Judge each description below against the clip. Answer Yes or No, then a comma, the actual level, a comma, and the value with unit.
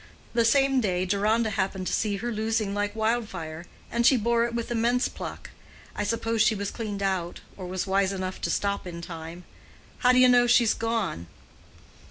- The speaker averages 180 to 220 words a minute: Yes, average, 190 wpm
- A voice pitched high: Yes, high, 215 Hz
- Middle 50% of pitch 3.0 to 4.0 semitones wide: Yes, average, 3.7 semitones